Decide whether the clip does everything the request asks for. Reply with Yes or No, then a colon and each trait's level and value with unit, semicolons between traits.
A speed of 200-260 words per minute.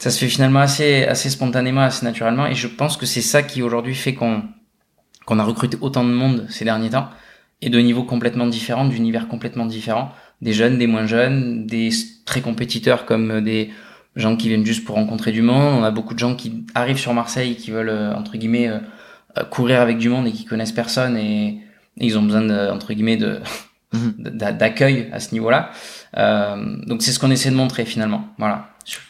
Yes: average, 205 wpm